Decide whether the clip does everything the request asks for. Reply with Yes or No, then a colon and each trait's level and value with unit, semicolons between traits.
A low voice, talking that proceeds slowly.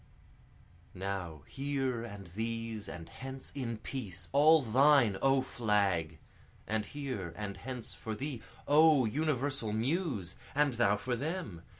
Yes: low, 115 Hz; slow, 125 wpm